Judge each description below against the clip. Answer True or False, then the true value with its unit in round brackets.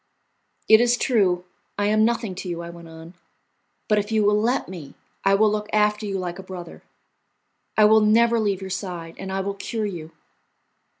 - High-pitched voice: True (200 Hz)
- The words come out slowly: False (195 wpm)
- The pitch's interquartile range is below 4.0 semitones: True (3.1 semitones)